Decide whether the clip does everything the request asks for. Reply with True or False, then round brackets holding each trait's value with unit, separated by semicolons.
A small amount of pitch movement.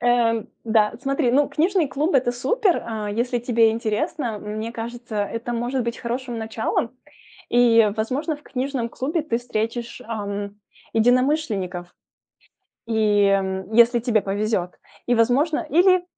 False (3.0 semitones)